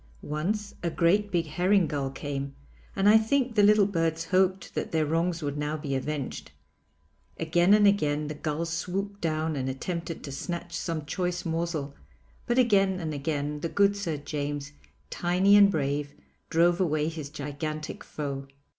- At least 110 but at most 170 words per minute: Yes, average, 165 wpm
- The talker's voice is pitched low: No, medium, 165 Hz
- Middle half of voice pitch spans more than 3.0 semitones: Yes, average, 4.3 semitones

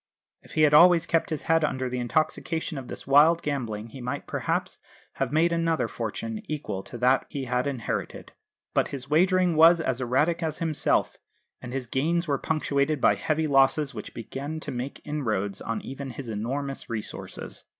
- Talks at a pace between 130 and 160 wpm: No, average, 180 wpm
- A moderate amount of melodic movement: Yes, average, 4.2 semitones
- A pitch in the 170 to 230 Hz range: No, medium, 140 Hz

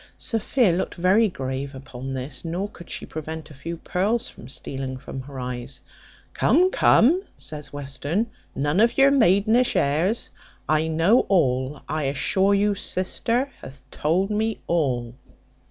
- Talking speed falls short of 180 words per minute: Yes, average, 145 wpm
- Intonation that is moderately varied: No, wide, 7.2 semitones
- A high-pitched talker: No, medium, 160 Hz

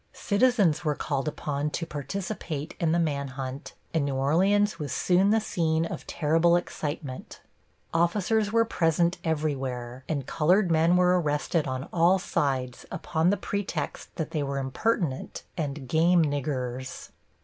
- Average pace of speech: Yes, average, 145 wpm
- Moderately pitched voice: Yes, medium, 160 Hz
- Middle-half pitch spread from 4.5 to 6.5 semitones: No, average, 4.1 semitones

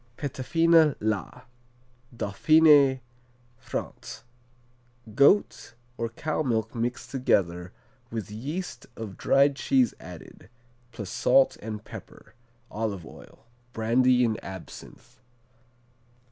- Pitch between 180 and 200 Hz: No, low, 120 Hz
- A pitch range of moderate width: Yes, average, 4.5 semitones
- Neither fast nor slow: No, slow, 90 wpm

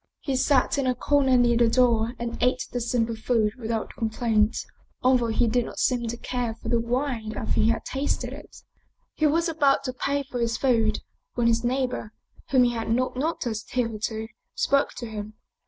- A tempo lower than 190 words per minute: No, average, 195 wpm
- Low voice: No, high, 240 Hz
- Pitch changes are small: Yes, narrow, 2.2 semitones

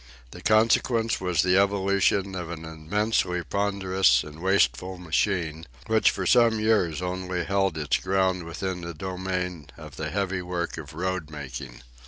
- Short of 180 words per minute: Yes, average, 145 wpm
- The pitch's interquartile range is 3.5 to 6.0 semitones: No, average, 3.0 semitones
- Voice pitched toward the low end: Yes, very low, 90 Hz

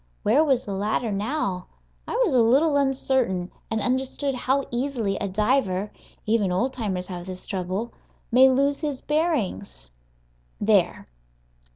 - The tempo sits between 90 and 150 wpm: Yes, average, 140 wpm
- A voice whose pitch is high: Yes, high, 235 Hz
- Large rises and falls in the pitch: Yes, wide, 5.8 semitones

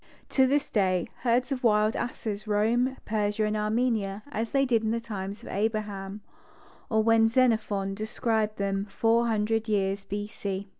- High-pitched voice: Yes, high, 215 Hz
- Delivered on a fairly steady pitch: Yes, narrow, 2.1 semitones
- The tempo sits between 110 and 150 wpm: No, average, 160 wpm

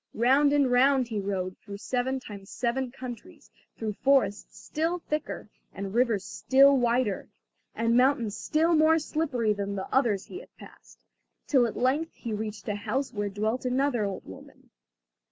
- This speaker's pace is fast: No, average, 160 wpm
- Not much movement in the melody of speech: No, average, 4.8 semitones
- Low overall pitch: No, high, 245 Hz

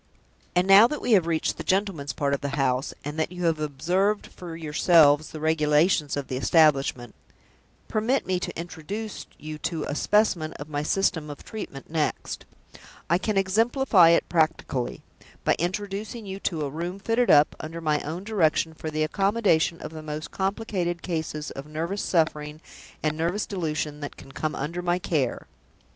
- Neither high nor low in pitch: Yes, medium, 165 Hz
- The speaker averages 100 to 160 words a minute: No, average, 175 wpm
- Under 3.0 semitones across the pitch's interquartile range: No, average, 4.1 semitones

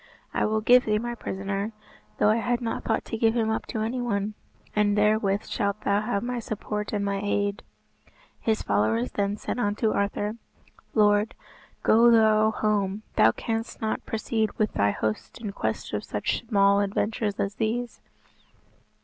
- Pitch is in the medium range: No, high, 215 Hz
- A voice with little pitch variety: Yes, narrow, 1.9 semitones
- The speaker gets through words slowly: No, average, 165 wpm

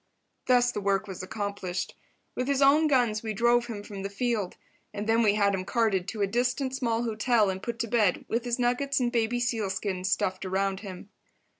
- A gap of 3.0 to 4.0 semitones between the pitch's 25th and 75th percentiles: Yes, average, 3.6 semitones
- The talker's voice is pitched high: Yes, high, 220 Hz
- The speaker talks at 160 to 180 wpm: No, fast, 205 wpm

